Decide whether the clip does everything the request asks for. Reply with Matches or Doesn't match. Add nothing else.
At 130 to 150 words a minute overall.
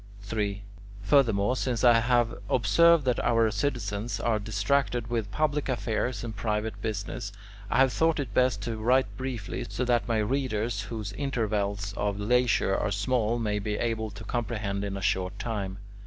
Doesn't match